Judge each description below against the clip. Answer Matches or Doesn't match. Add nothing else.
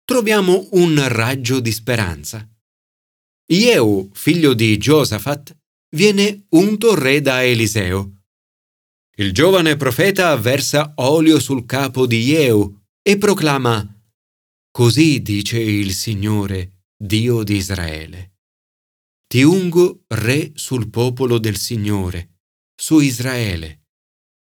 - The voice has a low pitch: Matches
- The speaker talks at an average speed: Doesn't match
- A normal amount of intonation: Doesn't match